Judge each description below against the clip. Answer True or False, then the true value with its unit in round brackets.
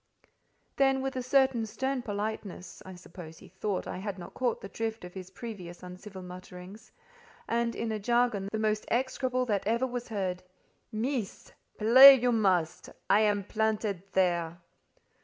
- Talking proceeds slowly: False (155 wpm)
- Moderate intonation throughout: True (4.3 semitones)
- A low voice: False (215 Hz)